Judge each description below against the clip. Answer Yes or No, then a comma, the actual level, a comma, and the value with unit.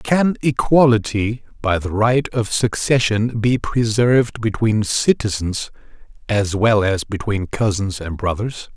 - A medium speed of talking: No, slow, 125 wpm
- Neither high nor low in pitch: No, low, 110 Hz